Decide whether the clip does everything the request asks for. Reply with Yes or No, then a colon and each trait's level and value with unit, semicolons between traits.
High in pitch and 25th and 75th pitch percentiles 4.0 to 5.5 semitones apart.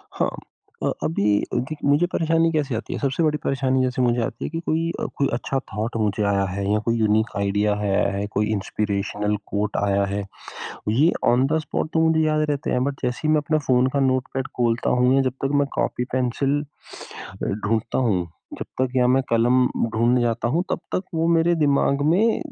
No: low, 125 Hz; average, 5.2 semitones